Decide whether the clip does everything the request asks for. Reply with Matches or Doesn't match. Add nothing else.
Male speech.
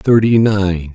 Matches